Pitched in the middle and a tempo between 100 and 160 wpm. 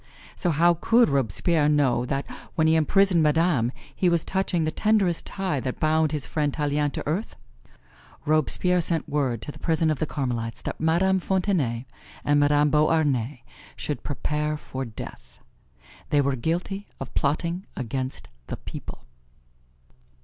Yes: medium, 150 Hz; average, 150 wpm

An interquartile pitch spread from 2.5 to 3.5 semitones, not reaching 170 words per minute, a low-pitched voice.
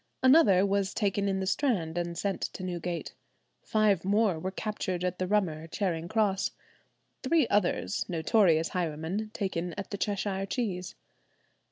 No: average, 3.0 semitones; average, 145 wpm; high, 190 Hz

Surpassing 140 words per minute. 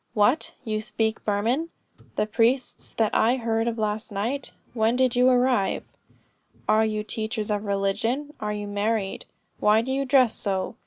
Yes: average, 160 wpm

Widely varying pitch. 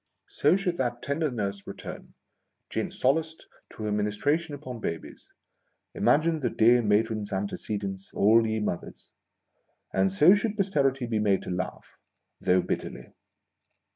Yes: wide, 6.5 semitones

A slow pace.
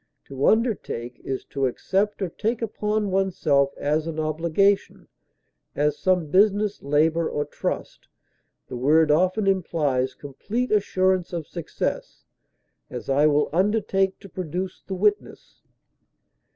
Yes: slow, 125 wpm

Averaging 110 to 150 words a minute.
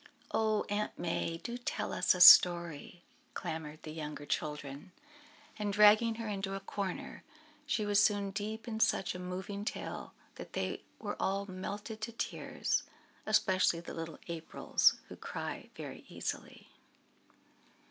Yes: average, 140 wpm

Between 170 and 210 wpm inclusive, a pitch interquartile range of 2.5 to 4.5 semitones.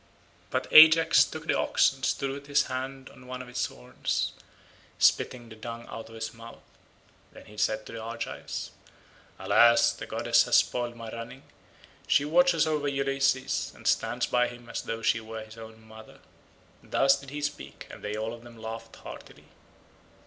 Yes: average, 180 wpm; average, 3.4 semitones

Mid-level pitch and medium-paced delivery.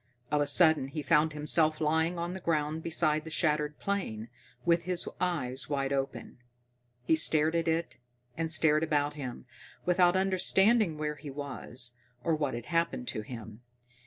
Yes: medium, 155 Hz; average, 160 wpm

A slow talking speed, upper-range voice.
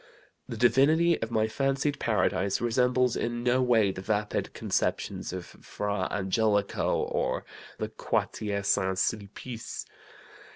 No: slow, 120 wpm; low, 110 Hz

